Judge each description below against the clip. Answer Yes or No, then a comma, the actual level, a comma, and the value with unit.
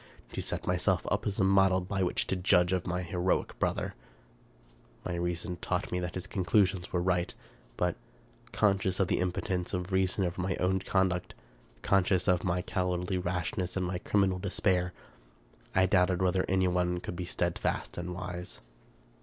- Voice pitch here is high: No, very low, 90 Hz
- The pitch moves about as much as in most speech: No, narrow, 1.1 semitones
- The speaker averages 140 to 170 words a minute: Yes, average, 165 wpm